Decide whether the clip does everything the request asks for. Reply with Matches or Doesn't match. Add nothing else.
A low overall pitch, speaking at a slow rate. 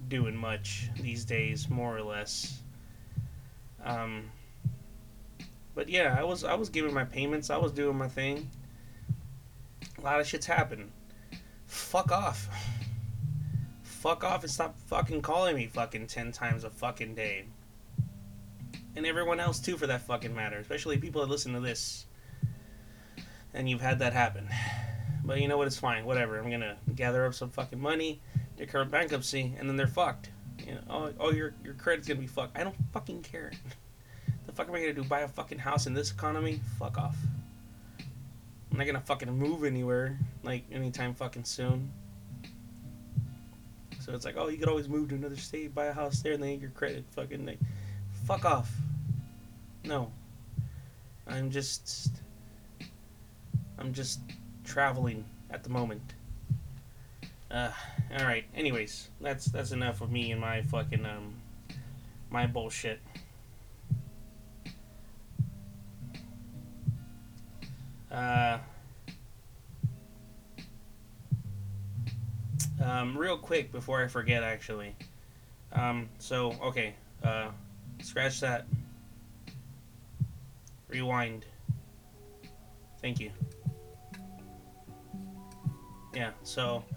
Matches